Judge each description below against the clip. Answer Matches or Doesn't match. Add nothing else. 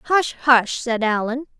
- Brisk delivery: Doesn't match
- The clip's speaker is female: Matches